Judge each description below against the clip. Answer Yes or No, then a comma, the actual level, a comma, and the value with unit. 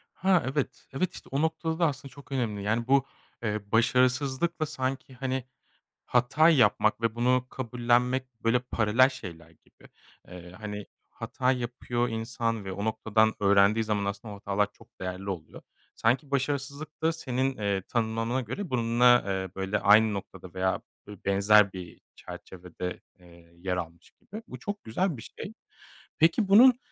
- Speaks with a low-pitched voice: Yes, low, 115 Hz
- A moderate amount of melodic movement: Yes, average, 4.7 semitones